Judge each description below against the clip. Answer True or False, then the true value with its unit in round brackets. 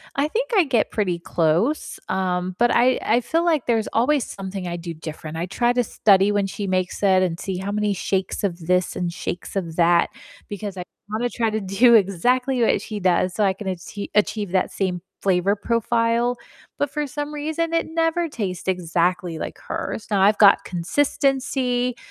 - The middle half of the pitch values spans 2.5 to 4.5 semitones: False (5.1 semitones)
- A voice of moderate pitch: False (205 Hz)